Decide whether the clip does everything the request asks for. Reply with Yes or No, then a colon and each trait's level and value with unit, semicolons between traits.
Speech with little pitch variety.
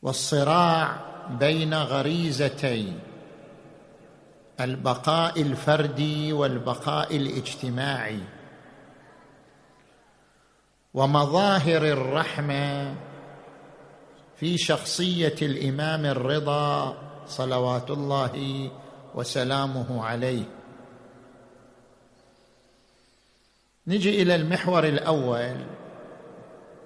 No: average, 3.2 semitones